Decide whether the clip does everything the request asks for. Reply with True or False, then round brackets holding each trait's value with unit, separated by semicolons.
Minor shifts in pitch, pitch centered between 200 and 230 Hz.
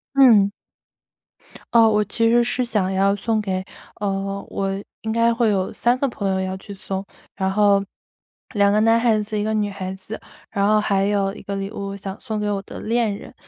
True (2.1 semitones; 205 Hz)